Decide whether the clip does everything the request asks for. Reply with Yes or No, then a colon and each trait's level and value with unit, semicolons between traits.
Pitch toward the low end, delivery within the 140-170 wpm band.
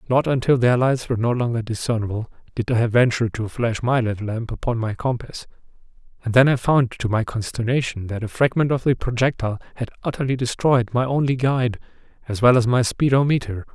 No: low, 120 Hz; average, 190 wpm